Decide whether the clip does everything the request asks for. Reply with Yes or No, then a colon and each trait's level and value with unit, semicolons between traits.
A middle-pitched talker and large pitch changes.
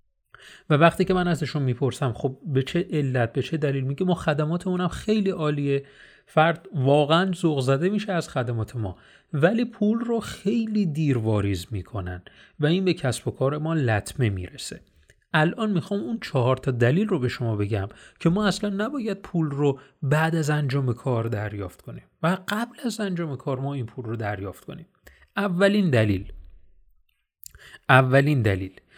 Yes: medium, 145 Hz; wide, 7.3 semitones